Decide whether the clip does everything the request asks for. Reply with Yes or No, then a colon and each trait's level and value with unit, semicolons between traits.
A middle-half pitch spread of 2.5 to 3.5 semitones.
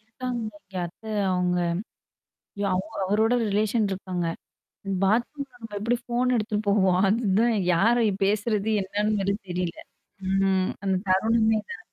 Yes: average, 2.9 semitones